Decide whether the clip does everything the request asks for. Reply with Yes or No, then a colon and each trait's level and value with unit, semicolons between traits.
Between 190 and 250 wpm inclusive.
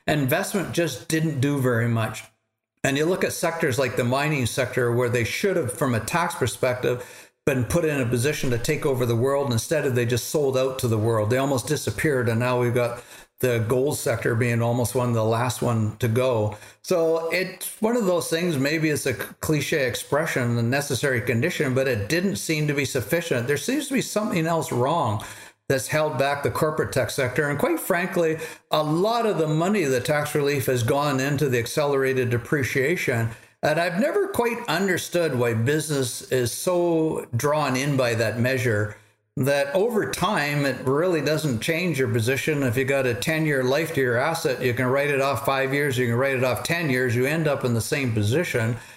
Yes: fast, 205 wpm